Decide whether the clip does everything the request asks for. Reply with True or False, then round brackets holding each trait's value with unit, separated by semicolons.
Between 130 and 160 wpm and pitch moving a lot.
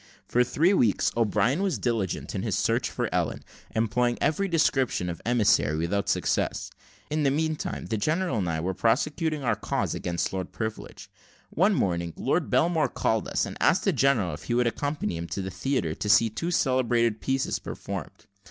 False (185 wpm; 6.6 semitones)